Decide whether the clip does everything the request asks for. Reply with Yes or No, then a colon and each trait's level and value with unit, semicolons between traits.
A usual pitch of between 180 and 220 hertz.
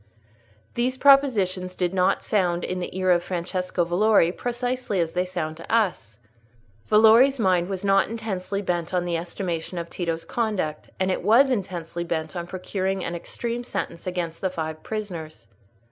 Yes: medium, 185 Hz